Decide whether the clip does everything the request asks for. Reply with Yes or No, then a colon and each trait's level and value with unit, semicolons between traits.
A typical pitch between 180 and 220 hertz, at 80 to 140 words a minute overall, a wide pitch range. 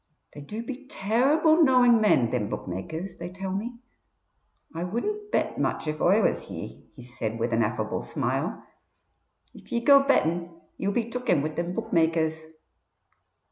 No: medium, 185 Hz; average, 165 wpm; wide, 7.4 semitones